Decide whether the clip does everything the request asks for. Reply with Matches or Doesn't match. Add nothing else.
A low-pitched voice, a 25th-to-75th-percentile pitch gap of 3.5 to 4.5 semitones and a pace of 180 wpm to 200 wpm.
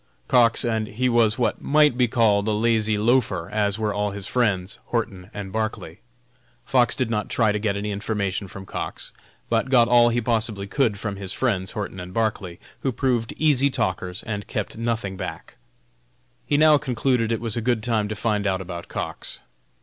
Doesn't match